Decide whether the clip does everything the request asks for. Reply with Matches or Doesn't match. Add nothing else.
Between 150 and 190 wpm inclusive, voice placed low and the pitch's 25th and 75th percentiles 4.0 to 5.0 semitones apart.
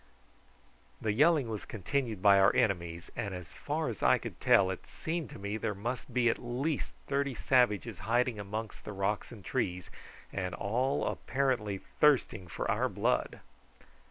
Matches